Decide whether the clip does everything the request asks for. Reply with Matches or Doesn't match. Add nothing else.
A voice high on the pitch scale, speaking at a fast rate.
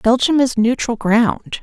Doesn't match